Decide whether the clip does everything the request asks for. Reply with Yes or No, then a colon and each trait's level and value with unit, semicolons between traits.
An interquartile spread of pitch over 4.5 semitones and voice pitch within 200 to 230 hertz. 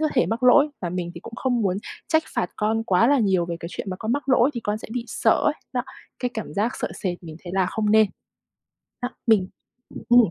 Yes: average, 4.9 semitones; high, 220 Hz